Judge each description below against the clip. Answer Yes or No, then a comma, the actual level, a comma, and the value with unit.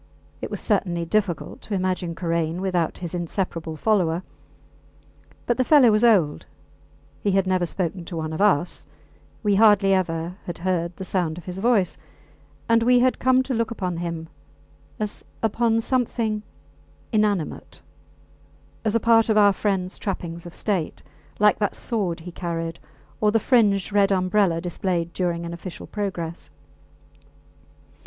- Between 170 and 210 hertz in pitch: Yes, high, 190 Hz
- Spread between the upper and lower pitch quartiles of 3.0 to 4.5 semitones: Yes, average, 3.8 semitones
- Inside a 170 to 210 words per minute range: No, average, 150 wpm